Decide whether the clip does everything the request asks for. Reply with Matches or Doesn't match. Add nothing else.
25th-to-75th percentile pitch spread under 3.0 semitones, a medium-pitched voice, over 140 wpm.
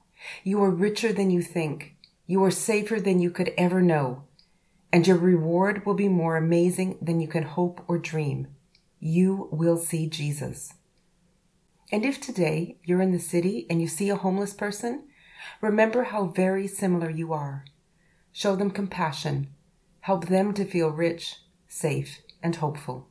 Matches